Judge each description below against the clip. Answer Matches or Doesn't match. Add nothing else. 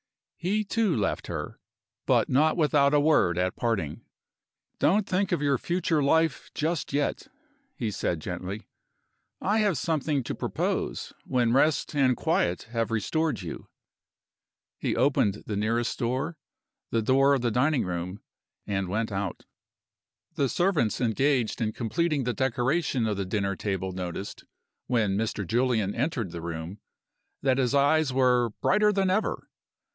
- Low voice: Matches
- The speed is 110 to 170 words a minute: Matches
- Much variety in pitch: Matches